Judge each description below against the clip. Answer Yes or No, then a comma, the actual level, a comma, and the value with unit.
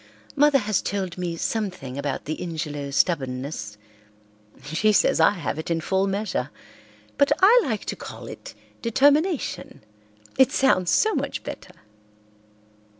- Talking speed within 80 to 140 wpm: Yes, slow, 135 wpm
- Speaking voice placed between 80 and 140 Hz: No, medium, 185 Hz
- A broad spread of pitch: Yes, wide, 7.8 semitones